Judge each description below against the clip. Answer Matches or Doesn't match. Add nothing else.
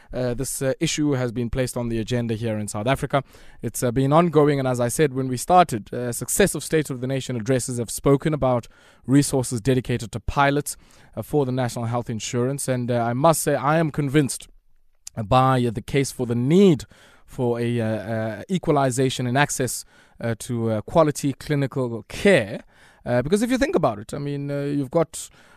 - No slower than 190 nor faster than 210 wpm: Matches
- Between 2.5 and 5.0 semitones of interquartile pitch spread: Matches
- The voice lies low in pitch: Matches